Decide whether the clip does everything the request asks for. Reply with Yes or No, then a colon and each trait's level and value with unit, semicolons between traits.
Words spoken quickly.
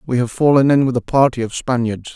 Yes: fast, 250 wpm